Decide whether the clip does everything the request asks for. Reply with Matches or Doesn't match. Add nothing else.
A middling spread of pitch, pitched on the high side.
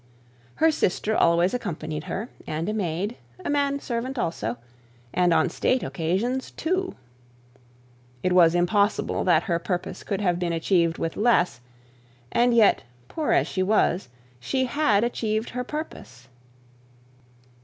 Doesn't match